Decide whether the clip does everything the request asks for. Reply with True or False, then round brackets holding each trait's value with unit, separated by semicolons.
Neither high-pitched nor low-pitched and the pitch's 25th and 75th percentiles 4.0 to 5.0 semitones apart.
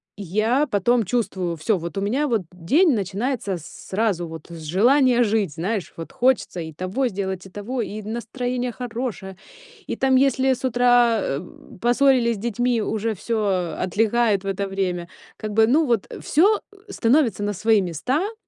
False (220 Hz; 4.5 semitones)